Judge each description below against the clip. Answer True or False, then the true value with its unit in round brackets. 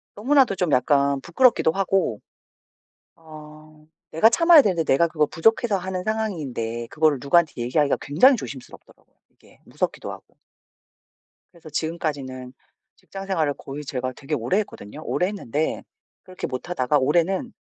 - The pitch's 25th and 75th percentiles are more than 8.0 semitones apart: False (5.5 semitones)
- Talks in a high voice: False (160 Hz)